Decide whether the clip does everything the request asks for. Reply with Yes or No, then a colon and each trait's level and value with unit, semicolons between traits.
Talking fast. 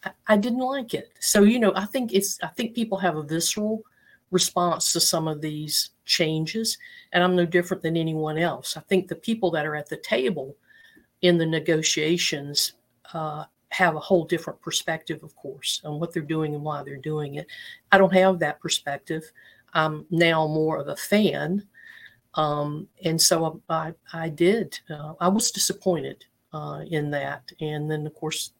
No: average, 185 wpm